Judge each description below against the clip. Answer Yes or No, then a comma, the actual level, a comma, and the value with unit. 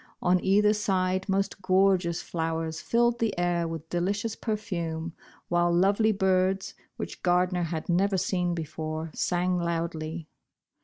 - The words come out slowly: Yes, slow, 125 wpm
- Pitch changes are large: No, narrow, 2.5 semitones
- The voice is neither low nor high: Yes, medium, 180 Hz